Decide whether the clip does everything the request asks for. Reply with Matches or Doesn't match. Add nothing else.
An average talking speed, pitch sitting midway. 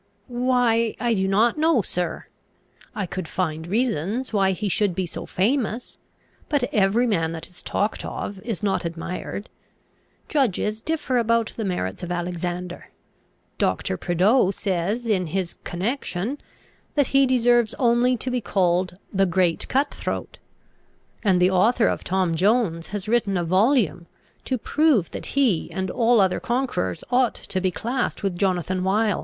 Doesn't match